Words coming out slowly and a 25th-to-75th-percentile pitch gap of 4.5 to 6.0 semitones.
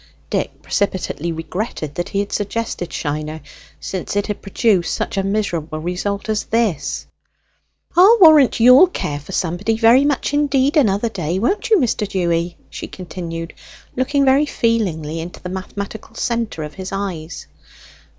No: average, 150 wpm; wide, 5.5 semitones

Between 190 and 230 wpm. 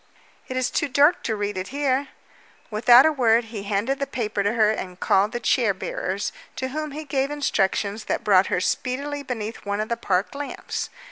Yes: average, 200 wpm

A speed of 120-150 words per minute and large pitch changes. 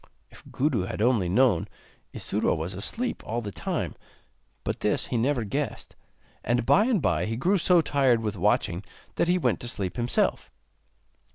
No: average, 170 wpm; wide, 6.0 semitones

